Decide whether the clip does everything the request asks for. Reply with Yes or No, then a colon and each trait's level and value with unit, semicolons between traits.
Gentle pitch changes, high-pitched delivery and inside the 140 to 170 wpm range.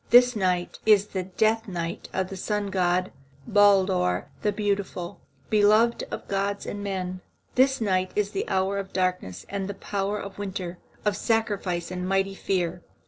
Yes: narrow, 2.0 semitones; high, 195 Hz; average, 160 wpm